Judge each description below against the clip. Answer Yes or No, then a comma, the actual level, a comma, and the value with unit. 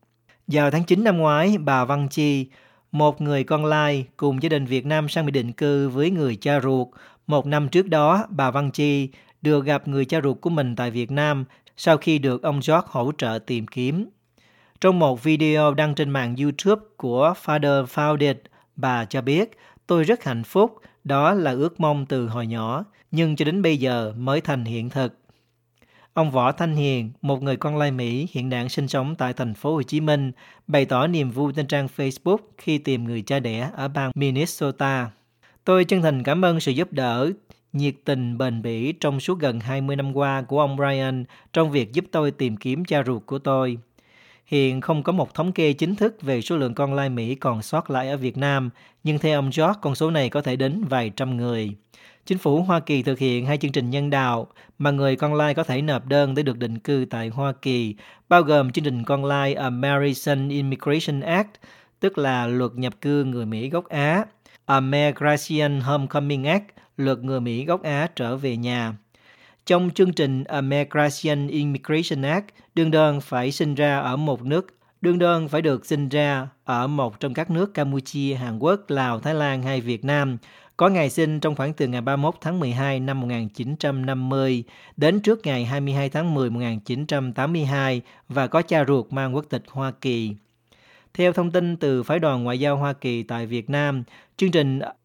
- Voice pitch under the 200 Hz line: Yes, medium, 140 Hz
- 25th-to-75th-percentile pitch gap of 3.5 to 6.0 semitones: No, average, 3.0 semitones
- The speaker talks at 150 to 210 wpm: Yes, average, 200 wpm